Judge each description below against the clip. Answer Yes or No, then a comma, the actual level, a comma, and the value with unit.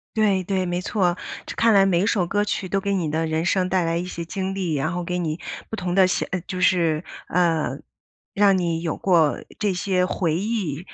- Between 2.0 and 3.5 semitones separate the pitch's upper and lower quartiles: Yes, narrow, 2.4 semitones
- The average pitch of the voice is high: No, medium, 180 Hz